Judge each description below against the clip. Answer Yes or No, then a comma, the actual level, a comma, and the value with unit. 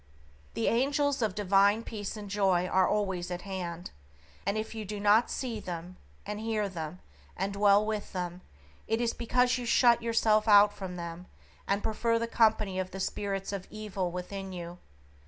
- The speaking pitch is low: No, high, 205 Hz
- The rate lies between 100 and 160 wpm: No, average, 175 wpm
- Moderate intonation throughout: Yes, average, 3.0 semitones